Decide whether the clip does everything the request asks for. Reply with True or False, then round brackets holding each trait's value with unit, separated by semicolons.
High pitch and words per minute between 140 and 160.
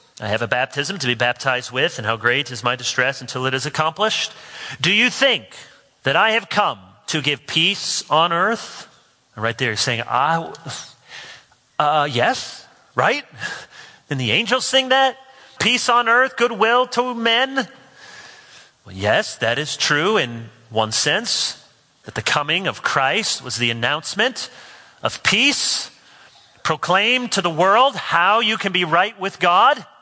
True (195 Hz; 155 wpm)